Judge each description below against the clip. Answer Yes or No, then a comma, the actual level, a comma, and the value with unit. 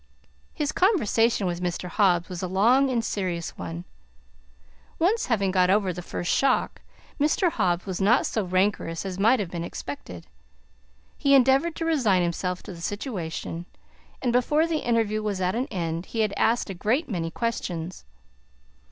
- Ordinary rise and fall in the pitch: No, wide, 5.7 semitones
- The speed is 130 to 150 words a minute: No, average, 165 wpm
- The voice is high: Yes, high, 200 Hz